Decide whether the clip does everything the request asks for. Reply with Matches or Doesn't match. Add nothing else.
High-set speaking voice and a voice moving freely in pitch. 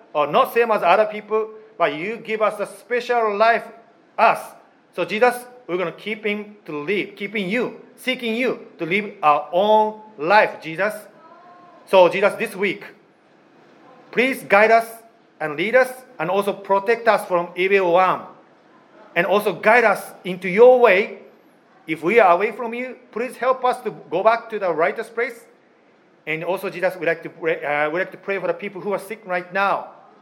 Doesn't match